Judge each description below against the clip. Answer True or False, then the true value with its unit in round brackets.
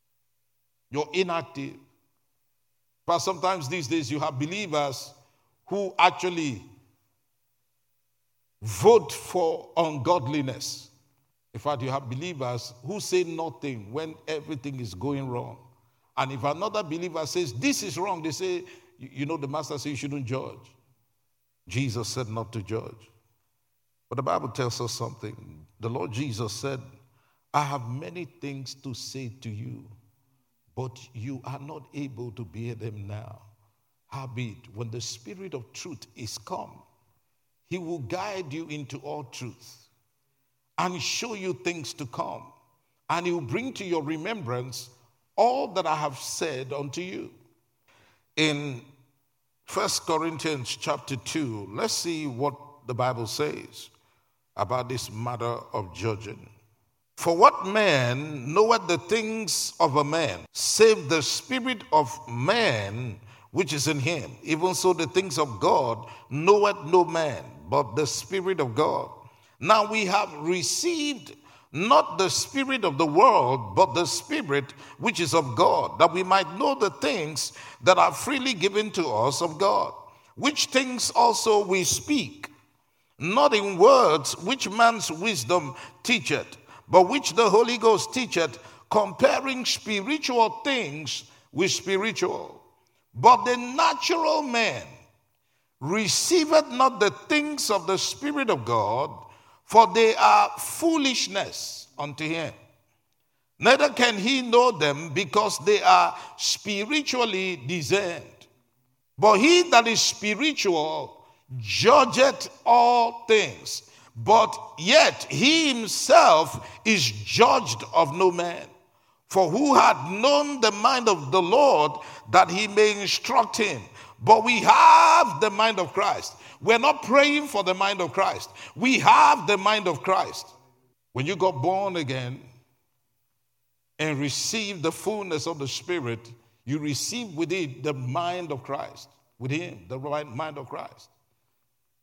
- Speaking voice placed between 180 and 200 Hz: False (155 Hz)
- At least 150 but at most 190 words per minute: False (135 wpm)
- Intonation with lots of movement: True (8.4 semitones)